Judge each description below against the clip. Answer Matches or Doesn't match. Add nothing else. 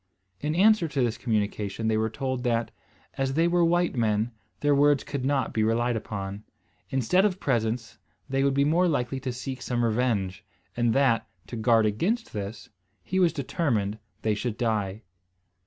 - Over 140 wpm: Matches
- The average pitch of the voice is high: Doesn't match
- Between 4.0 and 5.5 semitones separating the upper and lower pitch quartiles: Matches